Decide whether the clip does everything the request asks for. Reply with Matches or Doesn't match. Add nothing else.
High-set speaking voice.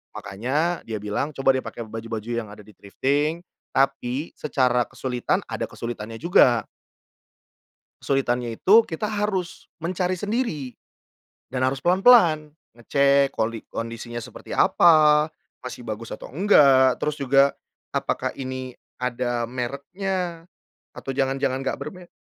Doesn't match